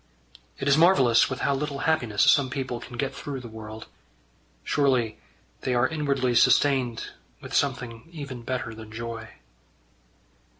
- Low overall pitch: Yes, low, 130 Hz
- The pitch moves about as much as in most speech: Yes, average, 3.2 semitones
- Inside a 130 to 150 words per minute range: Yes, average, 140 wpm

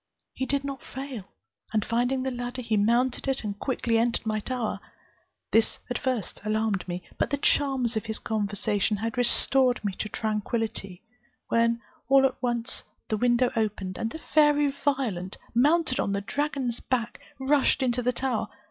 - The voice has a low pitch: No, high, 240 Hz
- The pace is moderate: Yes, average, 165 wpm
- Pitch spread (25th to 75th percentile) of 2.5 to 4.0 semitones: Yes, average, 3.5 semitones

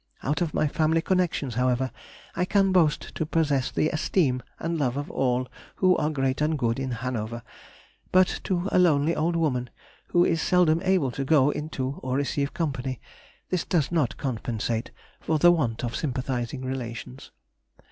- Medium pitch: Yes, medium, 145 Hz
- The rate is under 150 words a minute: No, average, 165 wpm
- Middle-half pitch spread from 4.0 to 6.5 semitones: Yes, average, 4.4 semitones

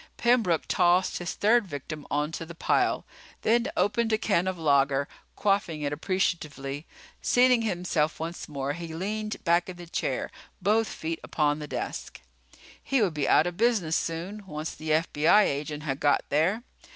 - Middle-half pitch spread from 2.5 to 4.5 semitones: No, average, 5.2 semitones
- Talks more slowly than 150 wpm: No, average, 165 wpm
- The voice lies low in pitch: No, medium, 170 Hz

